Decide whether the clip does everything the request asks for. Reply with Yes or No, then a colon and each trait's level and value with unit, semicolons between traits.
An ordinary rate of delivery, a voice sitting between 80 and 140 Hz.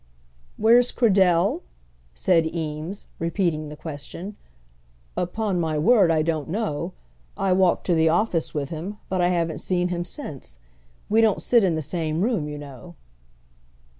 No: average, 150 wpm; medium, 170 Hz